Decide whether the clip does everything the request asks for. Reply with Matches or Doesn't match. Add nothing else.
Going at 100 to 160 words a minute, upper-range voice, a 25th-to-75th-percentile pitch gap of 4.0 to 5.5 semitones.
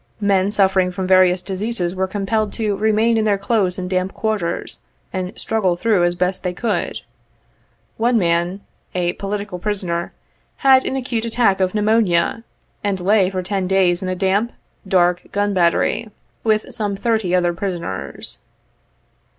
Doesn't match